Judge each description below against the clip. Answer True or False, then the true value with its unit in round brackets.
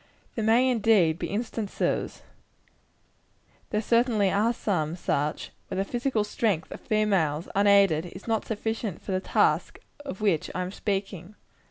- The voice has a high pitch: True (205 Hz)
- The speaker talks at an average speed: True (145 wpm)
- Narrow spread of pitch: False (3.4 semitones)